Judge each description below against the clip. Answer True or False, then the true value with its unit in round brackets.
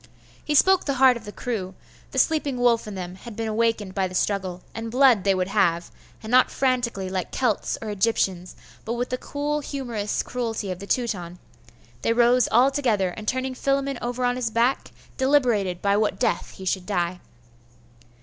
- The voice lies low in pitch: False (225 Hz)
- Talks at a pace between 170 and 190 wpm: True (185 wpm)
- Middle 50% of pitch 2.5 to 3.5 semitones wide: False (4.7 semitones)